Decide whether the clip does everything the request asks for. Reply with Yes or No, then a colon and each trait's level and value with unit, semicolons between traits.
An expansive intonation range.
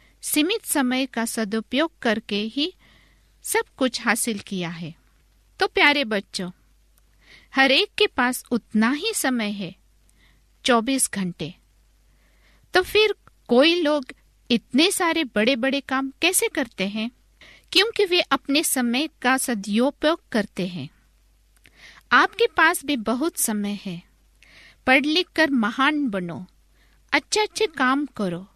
Yes: wide, 6.3 semitones